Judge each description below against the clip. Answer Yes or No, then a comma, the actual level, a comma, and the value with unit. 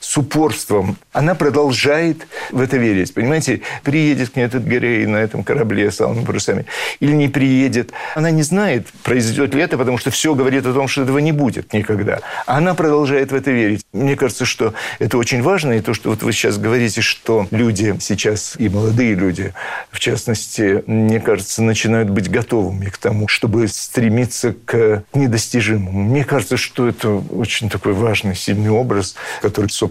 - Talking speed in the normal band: No, fast, 175 wpm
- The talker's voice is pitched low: Yes, low, 120 Hz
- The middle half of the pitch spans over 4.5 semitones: No, average, 4.1 semitones